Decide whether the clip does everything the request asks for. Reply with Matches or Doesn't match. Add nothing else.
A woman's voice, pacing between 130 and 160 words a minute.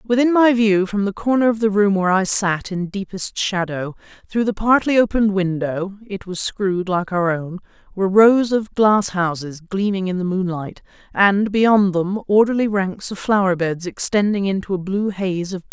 Doesn't match